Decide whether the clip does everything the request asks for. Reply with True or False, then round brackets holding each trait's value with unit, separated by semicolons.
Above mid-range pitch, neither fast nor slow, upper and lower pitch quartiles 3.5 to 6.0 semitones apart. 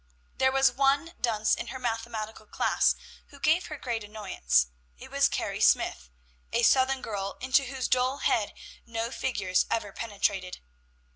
True (230 Hz; 150 wpm; 4.0 semitones)